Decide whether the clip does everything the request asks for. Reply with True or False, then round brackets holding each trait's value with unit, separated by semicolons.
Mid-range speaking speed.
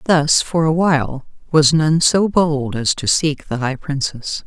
True (190 wpm)